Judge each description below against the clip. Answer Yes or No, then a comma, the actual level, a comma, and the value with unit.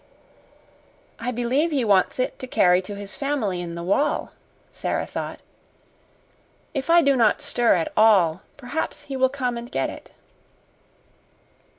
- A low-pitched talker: No, high, 240 Hz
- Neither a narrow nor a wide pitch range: No, wide, 5.8 semitones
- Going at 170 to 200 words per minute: No, average, 150 wpm